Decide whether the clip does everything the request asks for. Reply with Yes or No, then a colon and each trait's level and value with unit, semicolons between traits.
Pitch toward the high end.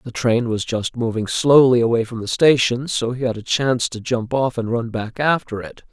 No: low, 120 Hz